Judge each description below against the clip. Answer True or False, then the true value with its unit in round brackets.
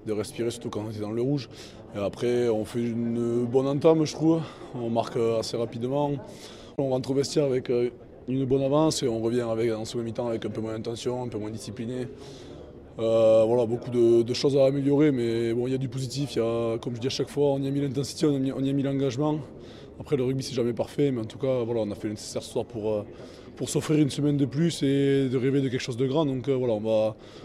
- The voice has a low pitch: True (125 Hz)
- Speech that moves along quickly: True (260 wpm)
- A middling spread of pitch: True (3.2 semitones)